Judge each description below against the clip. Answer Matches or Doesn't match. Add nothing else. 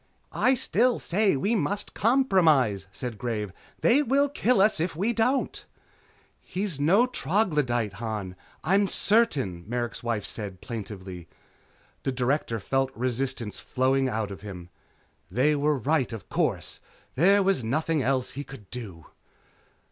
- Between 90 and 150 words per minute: Matches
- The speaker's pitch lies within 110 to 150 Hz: Matches